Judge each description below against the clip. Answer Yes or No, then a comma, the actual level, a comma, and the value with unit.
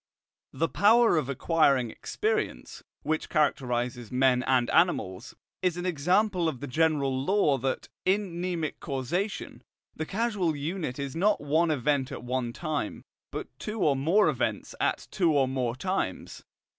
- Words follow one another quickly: No, average, 145 wpm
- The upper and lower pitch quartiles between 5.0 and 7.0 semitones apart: Yes, wide, 5.5 semitones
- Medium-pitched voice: Yes, medium, 155 Hz